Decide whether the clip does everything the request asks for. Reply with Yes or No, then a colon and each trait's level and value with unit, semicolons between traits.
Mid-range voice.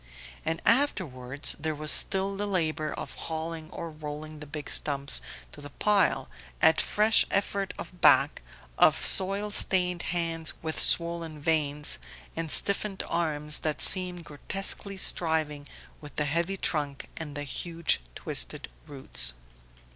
Yes: medium, 160 Hz